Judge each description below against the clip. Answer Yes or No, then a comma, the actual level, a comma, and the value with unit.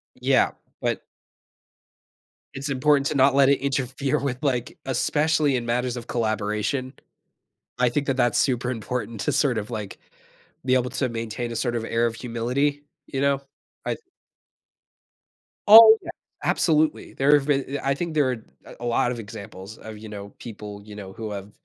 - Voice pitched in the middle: No, low, 125 Hz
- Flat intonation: No, average, 3.6 semitones